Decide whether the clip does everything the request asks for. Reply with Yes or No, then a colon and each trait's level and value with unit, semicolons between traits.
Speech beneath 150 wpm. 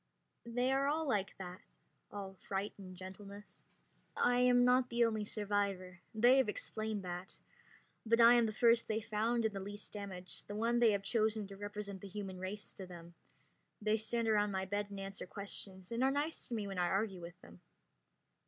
No: average, 190 wpm